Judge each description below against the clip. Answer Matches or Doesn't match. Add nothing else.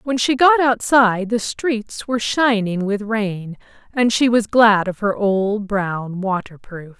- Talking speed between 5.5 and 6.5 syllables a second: Doesn't match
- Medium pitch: Doesn't match